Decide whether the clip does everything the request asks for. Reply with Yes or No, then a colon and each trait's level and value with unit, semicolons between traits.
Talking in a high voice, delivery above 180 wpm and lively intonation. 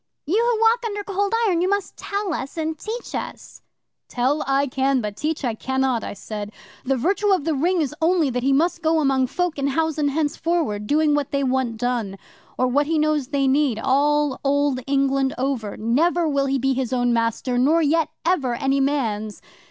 No: very high, 280 Hz; average, 200 wpm; average, 3.9 semitones